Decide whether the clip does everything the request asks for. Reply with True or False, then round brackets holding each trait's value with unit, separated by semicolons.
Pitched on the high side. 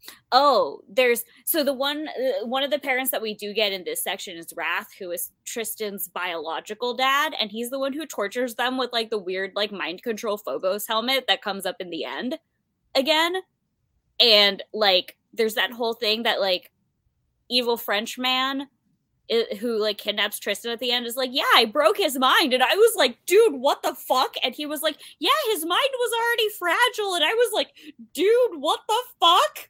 True (255 Hz)